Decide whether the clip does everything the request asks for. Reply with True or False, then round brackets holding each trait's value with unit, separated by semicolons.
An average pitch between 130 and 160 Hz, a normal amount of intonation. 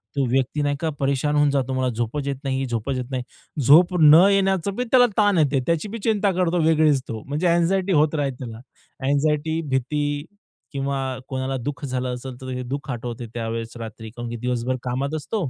True (140 Hz; 3.8 semitones)